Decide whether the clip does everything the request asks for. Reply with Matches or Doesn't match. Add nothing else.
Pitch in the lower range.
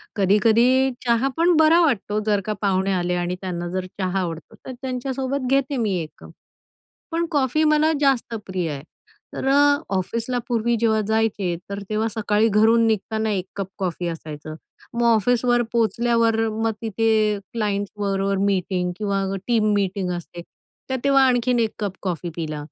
Doesn't match